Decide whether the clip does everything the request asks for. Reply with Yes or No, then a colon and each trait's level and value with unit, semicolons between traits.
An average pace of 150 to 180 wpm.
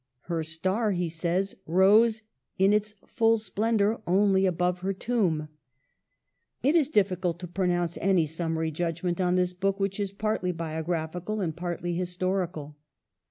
No: average, 140 wpm